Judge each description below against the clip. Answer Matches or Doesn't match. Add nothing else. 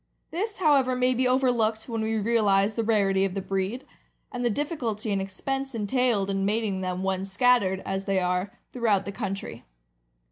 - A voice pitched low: Doesn't match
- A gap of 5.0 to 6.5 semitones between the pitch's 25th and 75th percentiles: Doesn't match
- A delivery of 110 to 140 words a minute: Doesn't match